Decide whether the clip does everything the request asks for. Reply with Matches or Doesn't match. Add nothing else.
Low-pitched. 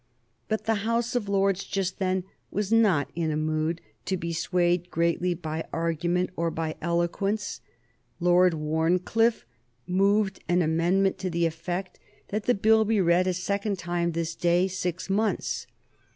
Doesn't match